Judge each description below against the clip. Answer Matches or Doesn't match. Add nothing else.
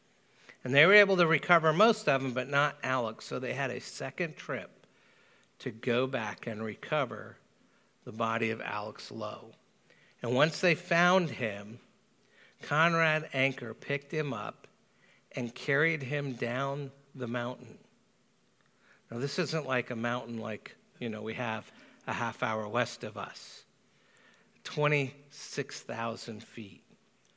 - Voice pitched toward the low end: Matches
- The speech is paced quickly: Doesn't match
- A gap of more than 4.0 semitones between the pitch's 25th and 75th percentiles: Matches